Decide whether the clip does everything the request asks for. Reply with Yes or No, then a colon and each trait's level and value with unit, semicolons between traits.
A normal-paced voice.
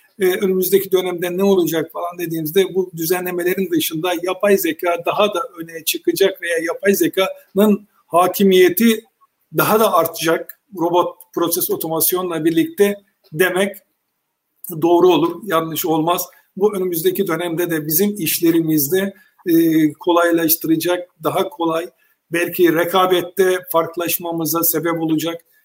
Yes: average, 110 wpm